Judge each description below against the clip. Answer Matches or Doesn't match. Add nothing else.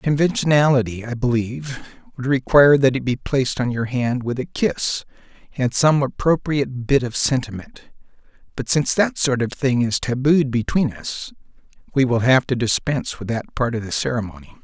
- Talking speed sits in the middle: Matches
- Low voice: Matches